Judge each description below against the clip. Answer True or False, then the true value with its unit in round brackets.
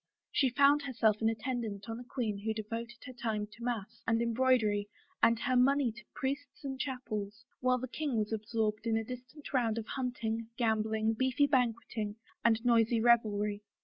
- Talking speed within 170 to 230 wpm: True (180 wpm)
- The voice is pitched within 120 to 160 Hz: False (230 Hz)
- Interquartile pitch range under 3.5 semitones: True (2.6 semitones)